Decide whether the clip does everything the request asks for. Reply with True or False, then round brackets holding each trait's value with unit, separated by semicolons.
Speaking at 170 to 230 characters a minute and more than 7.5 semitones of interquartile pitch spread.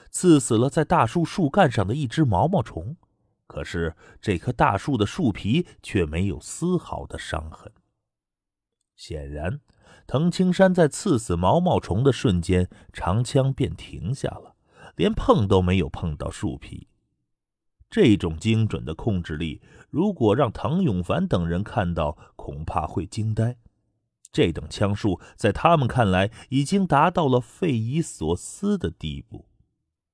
True (210 characters per minute; 8.0 semitones)